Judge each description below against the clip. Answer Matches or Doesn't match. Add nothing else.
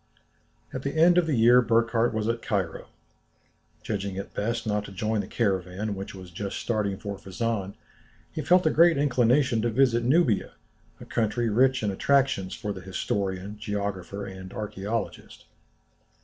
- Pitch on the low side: Matches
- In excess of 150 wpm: Matches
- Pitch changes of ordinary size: Matches